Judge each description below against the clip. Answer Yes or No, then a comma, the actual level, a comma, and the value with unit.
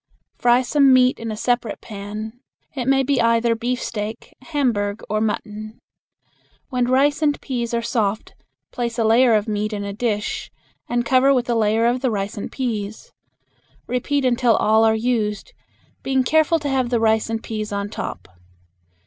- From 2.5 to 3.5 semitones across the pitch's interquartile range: Yes, average, 2.9 semitones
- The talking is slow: No, average, 170 wpm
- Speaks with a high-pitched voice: Yes, high, 235 Hz